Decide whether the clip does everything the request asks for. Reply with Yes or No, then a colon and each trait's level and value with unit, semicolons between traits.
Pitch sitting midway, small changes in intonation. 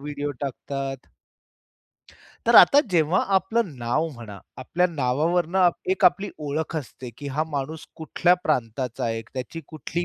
No: medium, 150 Hz; average, 4.8 semitones